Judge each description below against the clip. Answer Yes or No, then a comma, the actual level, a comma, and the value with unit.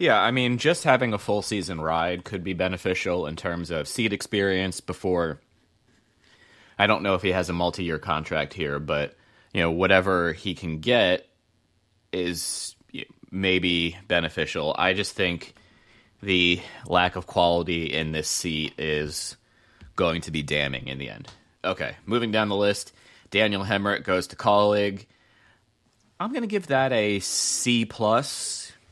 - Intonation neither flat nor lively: Yes, average, 3.5 semitones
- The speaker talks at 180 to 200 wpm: No, average, 155 wpm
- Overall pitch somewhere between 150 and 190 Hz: No, very low, 95 Hz